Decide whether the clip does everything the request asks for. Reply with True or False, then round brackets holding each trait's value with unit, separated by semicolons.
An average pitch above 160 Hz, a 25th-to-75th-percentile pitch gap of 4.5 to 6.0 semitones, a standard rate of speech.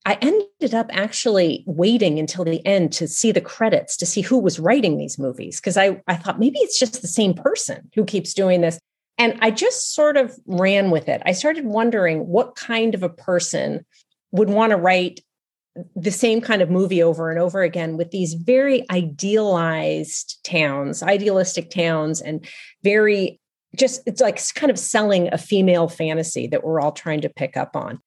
True (190 Hz; 4.8 semitones; 190 wpm)